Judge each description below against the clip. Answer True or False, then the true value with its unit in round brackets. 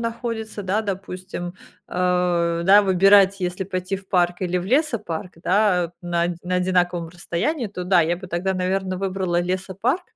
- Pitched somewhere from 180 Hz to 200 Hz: True (185 Hz)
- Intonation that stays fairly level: True (2.0 semitones)